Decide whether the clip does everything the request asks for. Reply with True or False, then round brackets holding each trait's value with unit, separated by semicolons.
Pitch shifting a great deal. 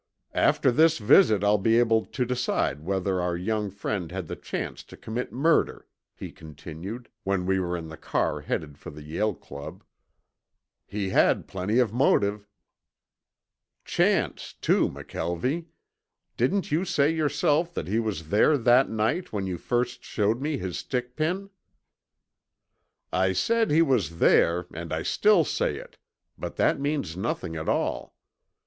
True (7.2 semitones)